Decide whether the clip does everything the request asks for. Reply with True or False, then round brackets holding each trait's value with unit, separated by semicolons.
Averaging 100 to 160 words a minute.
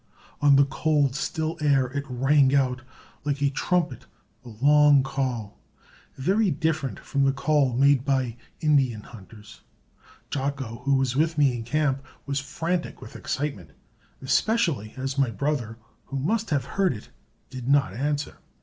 True (150 wpm)